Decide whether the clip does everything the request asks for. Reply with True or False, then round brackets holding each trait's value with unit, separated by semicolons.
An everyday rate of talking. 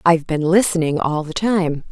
True (190 wpm)